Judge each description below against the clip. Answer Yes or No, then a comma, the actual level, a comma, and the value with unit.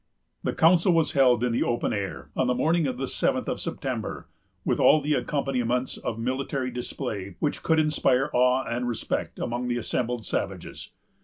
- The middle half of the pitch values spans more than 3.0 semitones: No, narrow, 2.4 semitones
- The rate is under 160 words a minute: No, average, 175 wpm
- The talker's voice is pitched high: No, low, 125 Hz